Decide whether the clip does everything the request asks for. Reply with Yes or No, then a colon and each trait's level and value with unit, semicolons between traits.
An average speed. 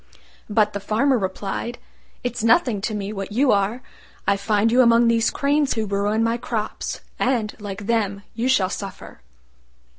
Yes: average, 160 wpm